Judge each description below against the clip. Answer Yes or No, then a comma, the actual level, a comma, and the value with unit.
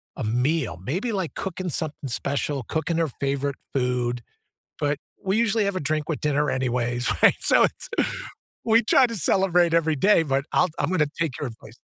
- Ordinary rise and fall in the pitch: No, wide, 5.7 semitones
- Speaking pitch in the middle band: Yes, medium, 150 Hz